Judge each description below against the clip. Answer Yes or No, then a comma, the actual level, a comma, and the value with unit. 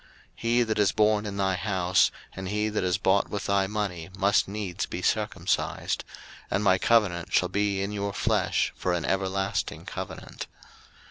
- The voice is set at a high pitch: No, low, 100 Hz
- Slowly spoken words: No, average, 175 wpm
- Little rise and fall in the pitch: Yes, narrow, 1.8 semitones